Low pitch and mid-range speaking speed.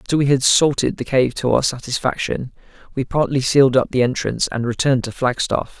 Yes: low, 130 Hz; average, 195 wpm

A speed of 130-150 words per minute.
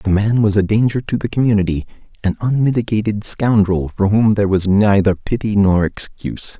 No: average, 175 wpm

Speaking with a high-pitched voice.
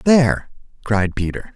No: low, 120 Hz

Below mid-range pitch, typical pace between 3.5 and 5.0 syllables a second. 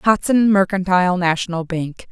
No: medium, 185 Hz; 4.9 syllables/s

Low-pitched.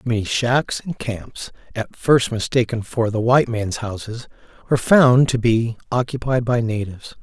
Yes: low, 115 Hz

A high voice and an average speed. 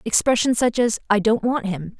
No: high, 225 Hz; fast, 210 wpm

